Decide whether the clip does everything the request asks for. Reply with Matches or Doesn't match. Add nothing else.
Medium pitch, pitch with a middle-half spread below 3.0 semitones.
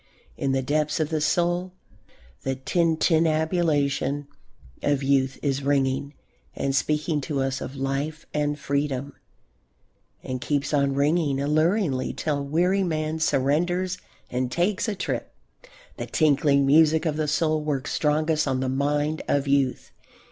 Matches